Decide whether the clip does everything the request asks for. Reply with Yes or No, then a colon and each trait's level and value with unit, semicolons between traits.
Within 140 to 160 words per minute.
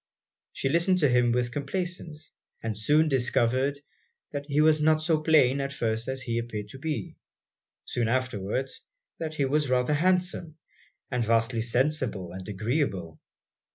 Yes: average, 150 wpm